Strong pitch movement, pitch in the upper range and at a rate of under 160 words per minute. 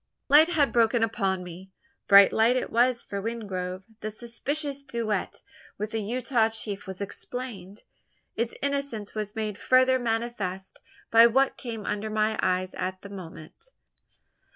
No: average, 3.6 semitones; high, 220 Hz; average, 145 wpm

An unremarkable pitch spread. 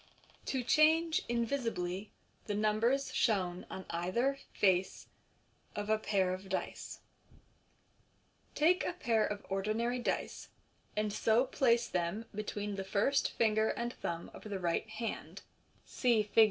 Yes: average, 3.6 semitones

